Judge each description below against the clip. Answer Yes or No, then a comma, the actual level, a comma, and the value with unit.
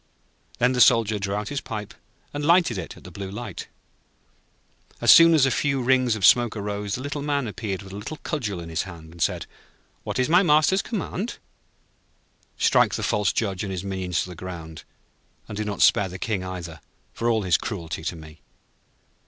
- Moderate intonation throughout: No, wide, 5.8 semitones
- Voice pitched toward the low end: Yes, low, 105 Hz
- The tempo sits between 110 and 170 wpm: No, average, 200 wpm